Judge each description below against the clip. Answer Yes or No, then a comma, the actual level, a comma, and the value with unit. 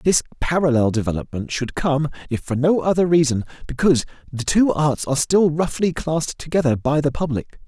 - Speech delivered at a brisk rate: No, average, 170 wpm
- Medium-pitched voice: Yes, medium, 145 Hz